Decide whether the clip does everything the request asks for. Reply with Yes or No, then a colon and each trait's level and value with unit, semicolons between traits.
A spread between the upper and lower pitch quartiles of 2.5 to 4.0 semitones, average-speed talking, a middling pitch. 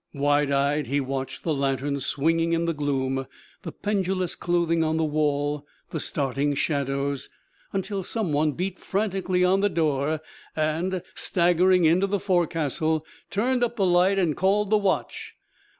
No: average, 4.5 semitones; average, 150 wpm; medium, 165 Hz